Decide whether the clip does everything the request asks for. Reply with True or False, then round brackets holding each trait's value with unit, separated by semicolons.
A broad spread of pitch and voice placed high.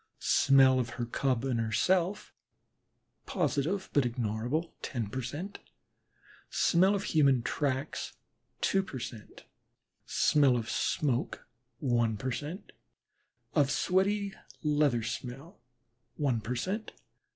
False (5.8 semitones; 135 Hz)